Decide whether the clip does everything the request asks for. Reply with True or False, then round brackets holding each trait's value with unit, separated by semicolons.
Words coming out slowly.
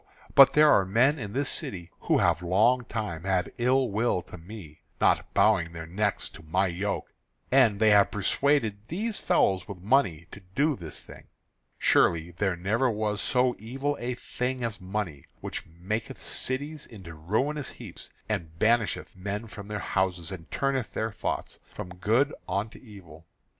False (165 wpm)